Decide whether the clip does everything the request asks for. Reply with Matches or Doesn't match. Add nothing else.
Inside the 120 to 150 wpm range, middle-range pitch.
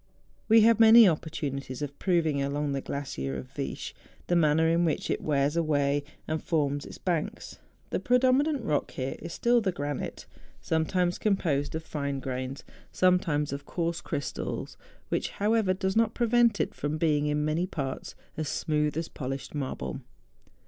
Doesn't match